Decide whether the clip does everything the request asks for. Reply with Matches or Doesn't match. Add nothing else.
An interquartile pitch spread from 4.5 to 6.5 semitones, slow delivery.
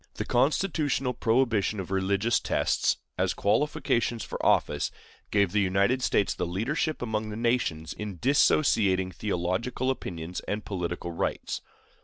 Matches